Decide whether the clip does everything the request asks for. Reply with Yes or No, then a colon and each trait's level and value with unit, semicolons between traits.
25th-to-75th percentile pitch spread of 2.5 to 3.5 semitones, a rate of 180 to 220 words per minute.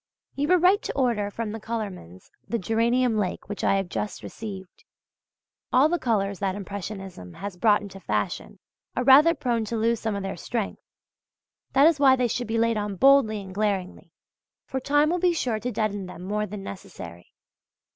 No: average, 4.2 semitones; average, 185 wpm